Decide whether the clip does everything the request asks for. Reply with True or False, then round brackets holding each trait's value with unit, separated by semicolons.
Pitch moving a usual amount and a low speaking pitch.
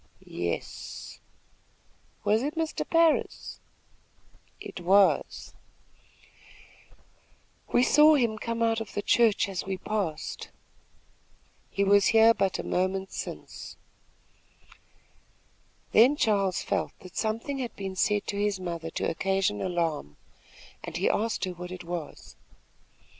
False (3.8 semitones; 200 Hz)